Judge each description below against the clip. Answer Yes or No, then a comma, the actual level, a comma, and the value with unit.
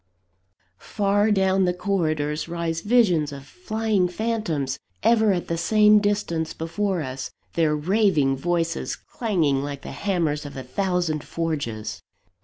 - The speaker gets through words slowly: Yes, slow, 130 wpm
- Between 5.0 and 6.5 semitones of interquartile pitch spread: Yes, average, 5.3 semitones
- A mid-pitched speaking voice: Yes, medium, 170 Hz